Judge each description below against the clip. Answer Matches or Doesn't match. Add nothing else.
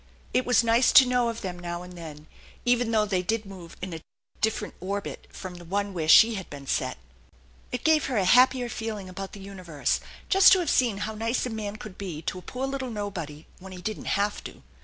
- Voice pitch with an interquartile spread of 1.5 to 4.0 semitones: Doesn't match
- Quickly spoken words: Matches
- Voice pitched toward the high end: Matches